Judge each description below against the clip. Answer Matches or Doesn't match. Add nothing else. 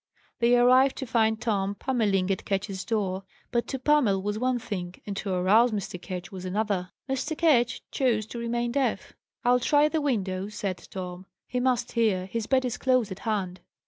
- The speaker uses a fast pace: Doesn't match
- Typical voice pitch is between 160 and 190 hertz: Doesn't match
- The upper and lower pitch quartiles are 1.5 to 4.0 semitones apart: Doesn't match